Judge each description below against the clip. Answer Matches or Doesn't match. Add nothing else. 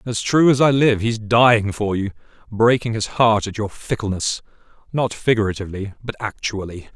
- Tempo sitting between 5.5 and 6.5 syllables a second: Doesn't match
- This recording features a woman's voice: Doesn't match